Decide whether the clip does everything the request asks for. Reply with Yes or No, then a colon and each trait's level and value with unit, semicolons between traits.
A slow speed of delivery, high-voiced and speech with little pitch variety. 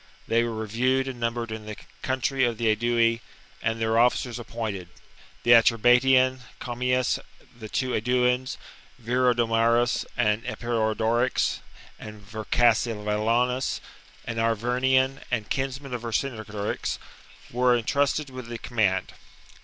No: slow, 120 wpm; low, 120 Hz; narrow, 2.2 semitones